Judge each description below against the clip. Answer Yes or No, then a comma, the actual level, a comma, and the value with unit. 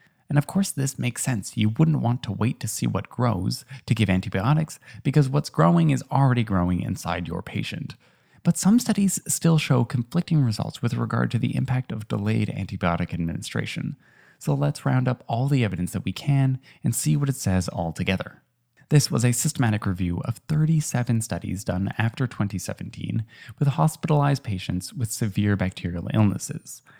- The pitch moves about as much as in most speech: No, wide, 6.4 semitones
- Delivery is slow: No, average, 175 wpm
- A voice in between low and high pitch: No, low, 120 Hz